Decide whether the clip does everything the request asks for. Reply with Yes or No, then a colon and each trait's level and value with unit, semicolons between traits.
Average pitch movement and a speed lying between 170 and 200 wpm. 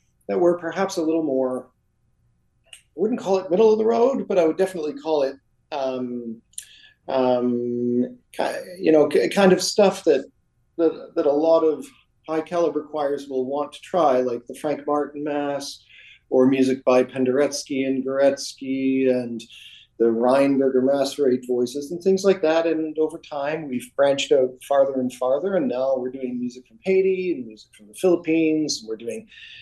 Yes: average, 4.2 semitones; average, 175 wpm